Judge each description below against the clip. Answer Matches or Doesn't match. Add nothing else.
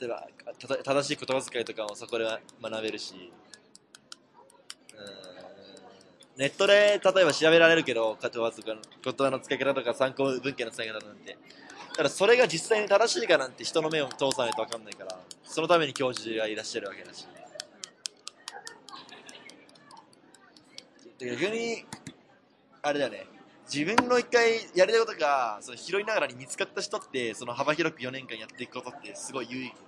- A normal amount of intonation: Doesn't match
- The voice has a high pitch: Doesn't match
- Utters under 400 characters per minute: Matches